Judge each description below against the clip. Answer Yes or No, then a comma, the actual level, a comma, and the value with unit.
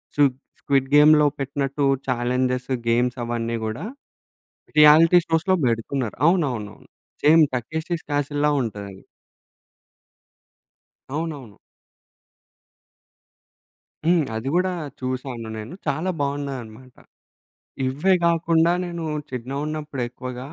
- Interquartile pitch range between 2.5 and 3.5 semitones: No, average, 4.1 semitones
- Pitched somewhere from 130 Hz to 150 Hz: Yes, medium, 140 Hz